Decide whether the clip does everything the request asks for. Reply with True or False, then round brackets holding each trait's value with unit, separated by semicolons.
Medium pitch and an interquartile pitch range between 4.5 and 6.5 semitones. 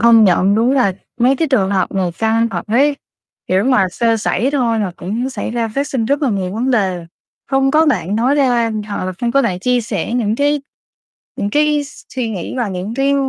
False (230 Hz; 4.9 semitones)